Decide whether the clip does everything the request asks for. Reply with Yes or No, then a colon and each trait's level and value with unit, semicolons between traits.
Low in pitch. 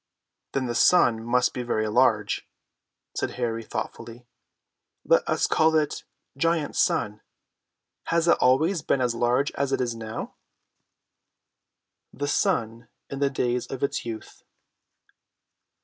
Yes: low, 125 Hz